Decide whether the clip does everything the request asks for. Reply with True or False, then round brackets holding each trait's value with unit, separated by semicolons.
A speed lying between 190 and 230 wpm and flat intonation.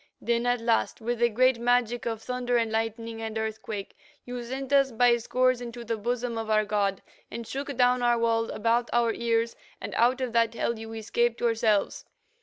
True (195 wpm; 1.5 semitones)